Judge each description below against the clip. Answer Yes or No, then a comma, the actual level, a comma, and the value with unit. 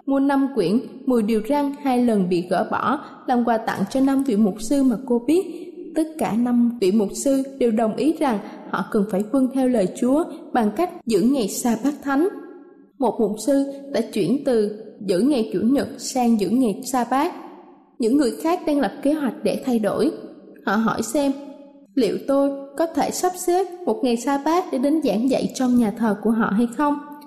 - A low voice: No, very high, 260 Hz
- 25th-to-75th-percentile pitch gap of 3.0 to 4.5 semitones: Yes, average, 4.1 semitones